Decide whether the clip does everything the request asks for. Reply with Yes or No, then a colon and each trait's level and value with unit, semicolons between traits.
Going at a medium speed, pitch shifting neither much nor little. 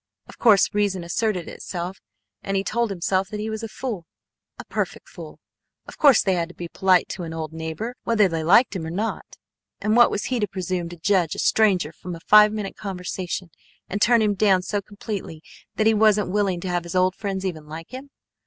No: fast, 220 wpm; average, 3.4 semitones